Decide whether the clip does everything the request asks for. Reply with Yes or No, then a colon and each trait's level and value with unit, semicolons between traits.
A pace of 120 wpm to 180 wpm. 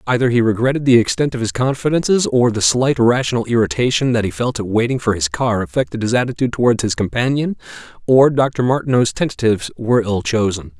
No: average, 190 wpm